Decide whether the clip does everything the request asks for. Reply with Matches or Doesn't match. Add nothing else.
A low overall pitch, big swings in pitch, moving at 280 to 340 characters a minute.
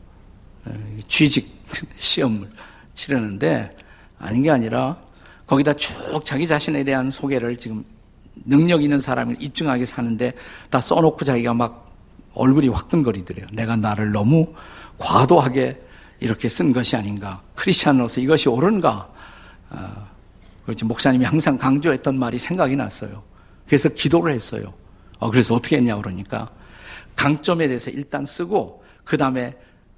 Matches